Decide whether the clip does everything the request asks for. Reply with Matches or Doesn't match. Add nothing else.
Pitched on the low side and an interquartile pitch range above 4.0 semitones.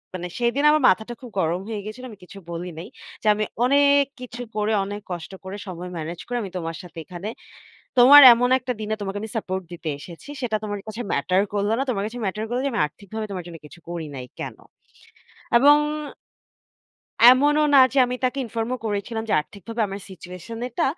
Doesn't match